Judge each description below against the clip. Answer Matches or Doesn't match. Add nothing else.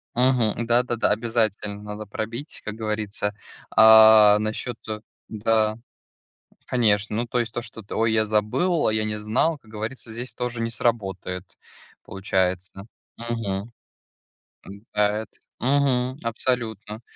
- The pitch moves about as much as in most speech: Doesn't match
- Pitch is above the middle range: Doesn't match